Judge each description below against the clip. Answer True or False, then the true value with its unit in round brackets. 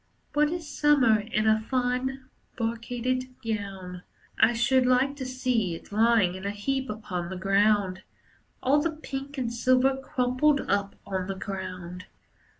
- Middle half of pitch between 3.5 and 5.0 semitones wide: True (4.7 semitones)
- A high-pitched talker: True (235 Hz)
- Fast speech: False (150 wpm)